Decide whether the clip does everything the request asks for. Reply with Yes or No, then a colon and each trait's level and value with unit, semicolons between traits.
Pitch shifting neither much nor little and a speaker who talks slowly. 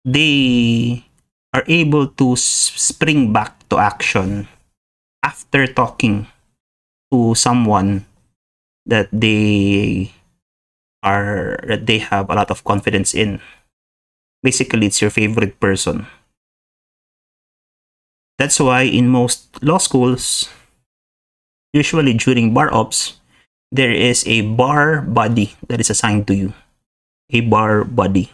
Yes: average, 4.1 semitones; slow, 110 wpm